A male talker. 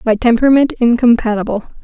No: female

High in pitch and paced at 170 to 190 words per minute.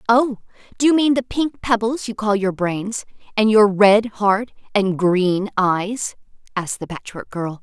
Yes: high, 210 Hz; average, 175 wpm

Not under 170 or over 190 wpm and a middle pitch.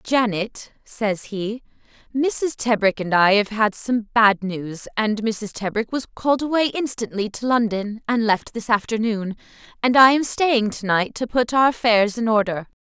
No: average, 175 wpm; high, 225 Hz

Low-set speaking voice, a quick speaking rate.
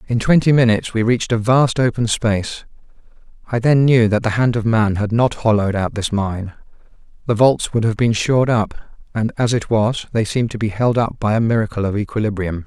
Yes: low, 110 Hz; fast, 215 wpm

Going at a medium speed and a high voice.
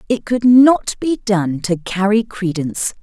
Yes: average, 160 wpm; high, 210 Hz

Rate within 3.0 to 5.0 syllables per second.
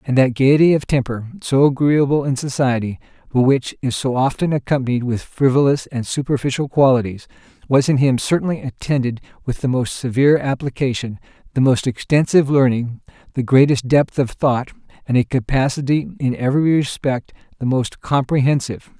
No: 5.4 syllables/s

